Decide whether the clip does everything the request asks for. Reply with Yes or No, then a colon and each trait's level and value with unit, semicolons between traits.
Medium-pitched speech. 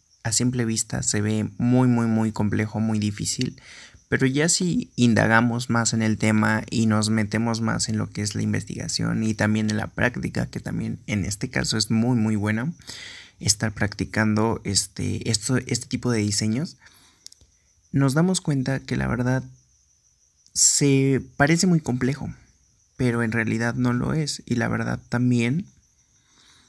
No: low, 115 Hz